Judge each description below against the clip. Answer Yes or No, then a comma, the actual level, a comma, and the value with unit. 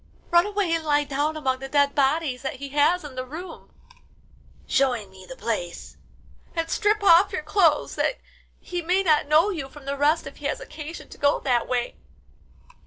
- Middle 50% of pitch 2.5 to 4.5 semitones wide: Yes, average, 4.2 semitones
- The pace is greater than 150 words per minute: Yes, average, 190 wpm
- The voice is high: Yes, very high, 295 Hz